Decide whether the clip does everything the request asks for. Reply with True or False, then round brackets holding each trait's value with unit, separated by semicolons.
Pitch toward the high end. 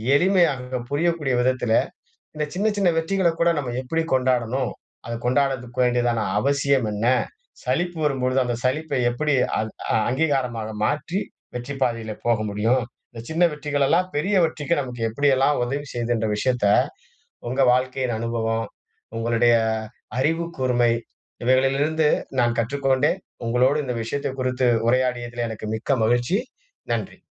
False (130 Hz)